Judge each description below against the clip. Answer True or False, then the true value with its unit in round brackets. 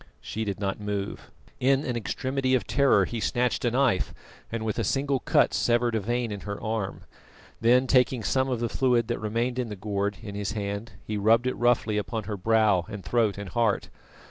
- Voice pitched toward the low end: True (115 Hz)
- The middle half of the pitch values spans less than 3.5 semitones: True (3.1 semitones)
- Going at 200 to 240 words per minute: True (205 wpm)